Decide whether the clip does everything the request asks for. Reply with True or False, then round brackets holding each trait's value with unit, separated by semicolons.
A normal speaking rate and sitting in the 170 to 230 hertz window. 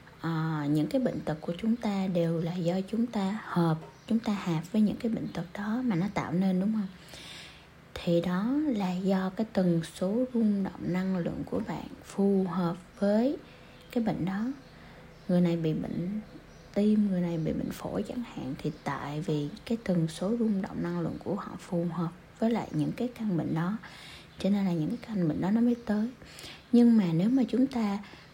True (210 wpm; 190 Hz)